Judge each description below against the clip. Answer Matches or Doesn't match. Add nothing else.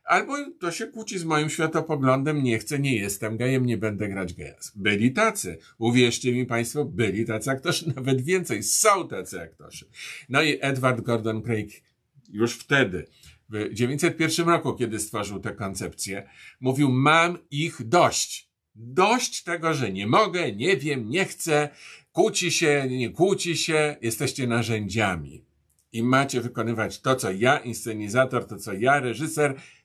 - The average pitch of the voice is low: Matches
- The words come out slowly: Doesn't match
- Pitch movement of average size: Doesn't match